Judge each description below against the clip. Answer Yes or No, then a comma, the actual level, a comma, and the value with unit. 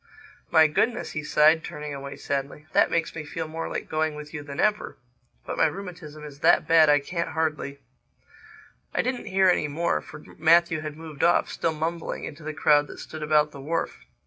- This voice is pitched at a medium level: Yes, medium, 155 Hz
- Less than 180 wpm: No, average, 195 wpm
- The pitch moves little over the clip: Yes, narrow, 1.9 semitones